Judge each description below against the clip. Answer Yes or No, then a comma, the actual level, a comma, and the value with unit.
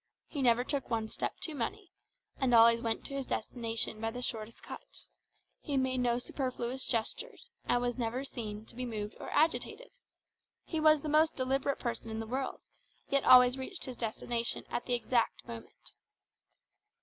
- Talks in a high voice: Yes, high, 245 Hz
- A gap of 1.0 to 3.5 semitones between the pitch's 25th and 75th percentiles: Yes, average, 2.9 semitones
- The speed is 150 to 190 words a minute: Yes, average, 175 wpm